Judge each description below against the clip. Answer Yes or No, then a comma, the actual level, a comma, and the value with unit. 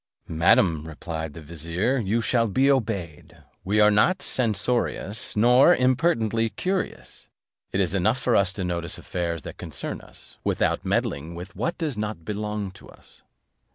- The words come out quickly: No, average, 155 wpm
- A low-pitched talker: Yes, low, 105 Hz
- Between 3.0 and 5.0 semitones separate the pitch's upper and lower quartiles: No, wide, 5.6 semitones